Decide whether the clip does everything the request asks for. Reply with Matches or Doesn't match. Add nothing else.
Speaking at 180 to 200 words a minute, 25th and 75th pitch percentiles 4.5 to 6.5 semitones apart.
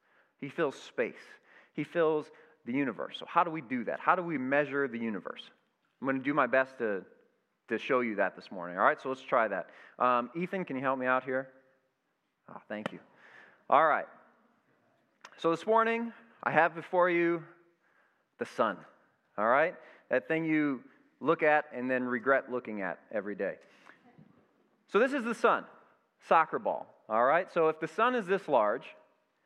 Matches